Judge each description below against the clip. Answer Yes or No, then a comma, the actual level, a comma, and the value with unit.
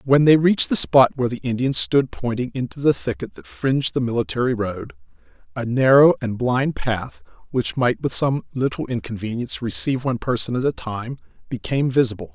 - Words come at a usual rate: Yes, average, 180 wpm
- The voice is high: No, low, 120 Hz